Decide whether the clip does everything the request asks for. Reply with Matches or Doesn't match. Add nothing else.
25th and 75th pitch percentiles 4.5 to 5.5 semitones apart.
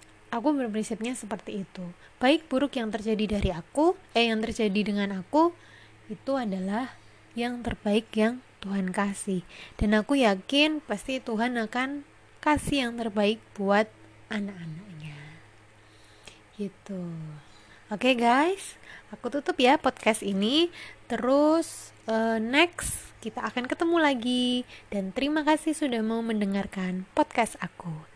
Matches